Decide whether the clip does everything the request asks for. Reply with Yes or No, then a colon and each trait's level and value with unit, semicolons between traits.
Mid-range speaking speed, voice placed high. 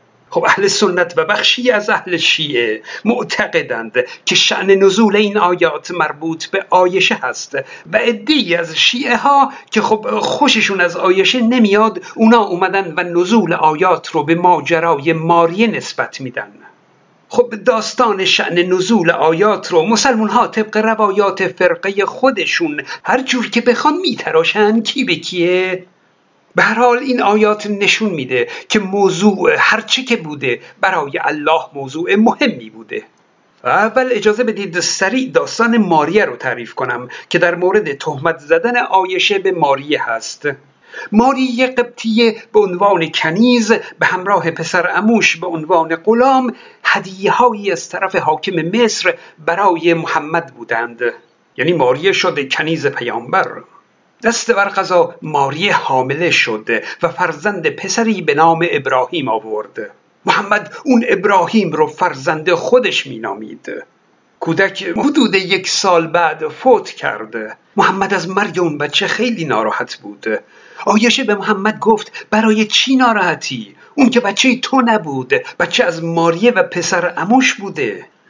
Yes: average, 135 wpm; high, 210 Hz